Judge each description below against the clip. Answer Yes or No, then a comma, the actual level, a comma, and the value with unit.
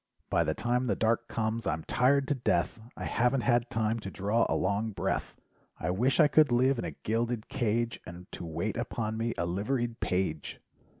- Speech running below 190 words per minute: No, average, 195 wpm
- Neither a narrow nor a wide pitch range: Yes, average, 3.8 semitones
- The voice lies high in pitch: No, low, 115 Hz